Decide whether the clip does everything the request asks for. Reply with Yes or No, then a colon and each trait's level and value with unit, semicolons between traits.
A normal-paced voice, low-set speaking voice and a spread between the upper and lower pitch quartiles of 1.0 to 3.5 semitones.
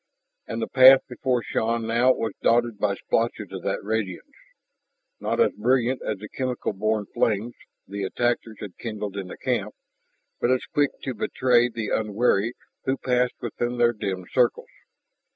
Yes: average, 160 wpm; low, 115 Hz; average, 2.9 semitones